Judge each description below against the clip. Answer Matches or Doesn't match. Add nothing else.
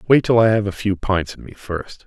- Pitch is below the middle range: Matches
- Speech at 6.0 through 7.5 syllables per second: Doesn't match